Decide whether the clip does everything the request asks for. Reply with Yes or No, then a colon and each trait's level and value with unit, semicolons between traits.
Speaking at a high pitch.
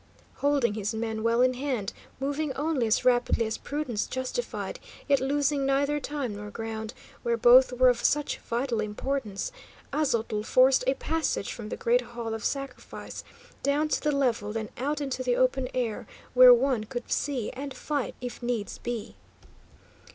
Yes: very high, 250 Hz